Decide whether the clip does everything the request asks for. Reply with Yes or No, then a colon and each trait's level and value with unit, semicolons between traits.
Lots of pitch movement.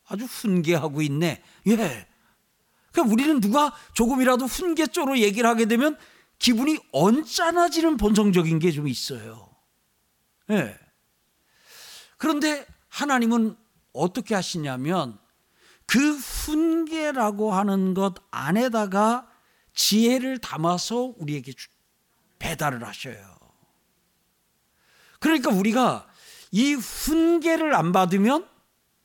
Yes: wide, 8.2 semitones